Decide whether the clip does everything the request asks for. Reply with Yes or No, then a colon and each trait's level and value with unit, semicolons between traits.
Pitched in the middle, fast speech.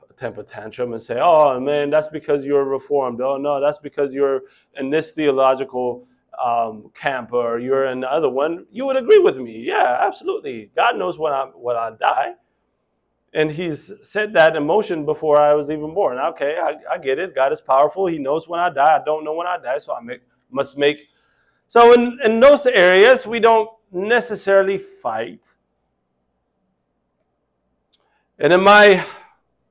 No: medium, 150 Hz; average, 175 wpm